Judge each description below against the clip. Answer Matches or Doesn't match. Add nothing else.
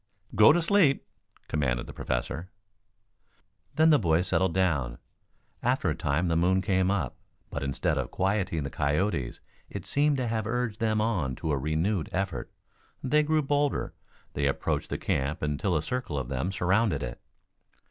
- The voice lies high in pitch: Doesn't match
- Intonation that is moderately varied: Doesn't match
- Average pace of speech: Matches